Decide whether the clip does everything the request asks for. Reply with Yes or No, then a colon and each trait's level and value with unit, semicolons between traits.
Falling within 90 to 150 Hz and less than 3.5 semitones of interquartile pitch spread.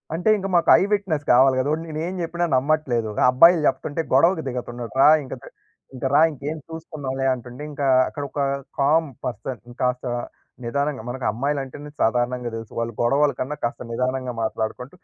No: low, 135 Hz; average, 3.9 semitones